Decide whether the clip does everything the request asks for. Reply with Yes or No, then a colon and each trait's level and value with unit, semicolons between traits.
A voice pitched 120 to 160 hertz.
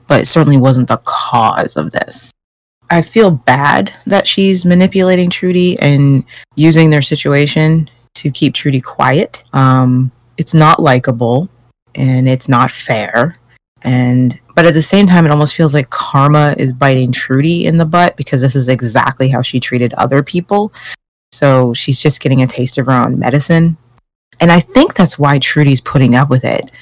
Yes: medium, 140 Hz